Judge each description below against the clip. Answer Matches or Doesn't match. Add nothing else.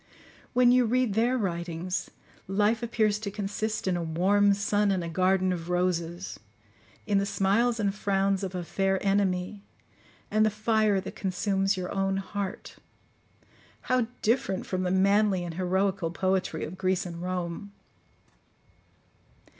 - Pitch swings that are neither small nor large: Doesn't match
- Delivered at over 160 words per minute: Doesn't match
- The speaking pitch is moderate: Doesn't match